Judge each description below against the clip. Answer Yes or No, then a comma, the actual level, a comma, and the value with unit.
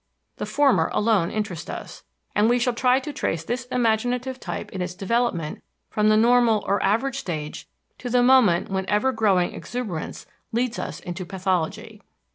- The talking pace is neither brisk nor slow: Yes, average, 165 wpm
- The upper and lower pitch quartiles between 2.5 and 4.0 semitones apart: No, average, 4.7 semitones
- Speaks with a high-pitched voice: Yes, high, 220 Hz